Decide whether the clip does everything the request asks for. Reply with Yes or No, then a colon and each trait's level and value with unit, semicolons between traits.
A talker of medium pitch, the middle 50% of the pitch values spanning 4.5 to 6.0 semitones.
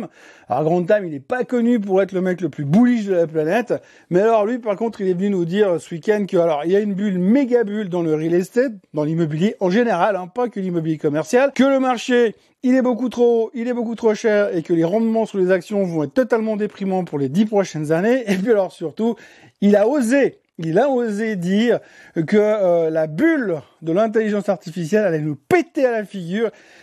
No: high, 205 Hz; average, 5.2 semitones